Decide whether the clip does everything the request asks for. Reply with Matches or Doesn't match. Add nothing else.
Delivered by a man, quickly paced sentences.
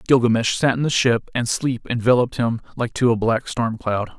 Matches